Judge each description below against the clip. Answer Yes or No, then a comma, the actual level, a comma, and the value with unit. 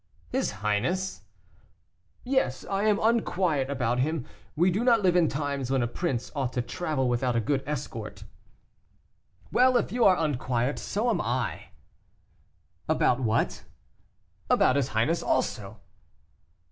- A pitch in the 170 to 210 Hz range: No, medium, 140 Hz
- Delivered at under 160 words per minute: Yes, slow, 135 wpm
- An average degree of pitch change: No, wide, 7.2 semitones